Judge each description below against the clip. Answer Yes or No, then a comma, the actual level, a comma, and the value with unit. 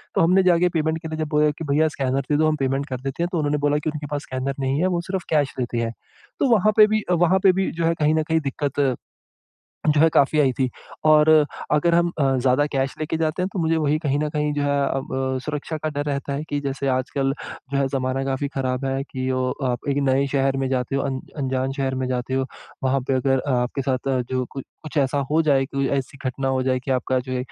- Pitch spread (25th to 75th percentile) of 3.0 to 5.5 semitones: No, narrow, 2.6 semitones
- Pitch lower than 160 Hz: Yes, medium, 140 Hz